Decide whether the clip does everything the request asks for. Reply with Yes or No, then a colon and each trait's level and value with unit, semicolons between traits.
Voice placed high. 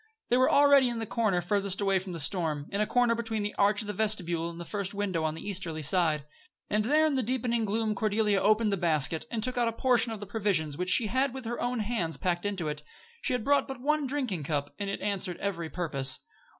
Yes: high, 205 Hz